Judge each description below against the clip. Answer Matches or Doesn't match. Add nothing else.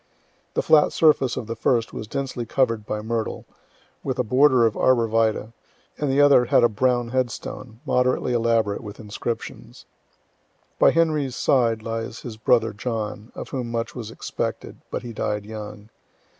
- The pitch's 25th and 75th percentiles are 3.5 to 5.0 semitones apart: Doesn't match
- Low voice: Matches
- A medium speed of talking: Matches